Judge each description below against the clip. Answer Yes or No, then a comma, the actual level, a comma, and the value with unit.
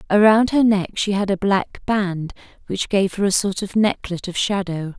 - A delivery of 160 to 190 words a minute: No, fast, 205 wpm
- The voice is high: Yes, high, 195 Hz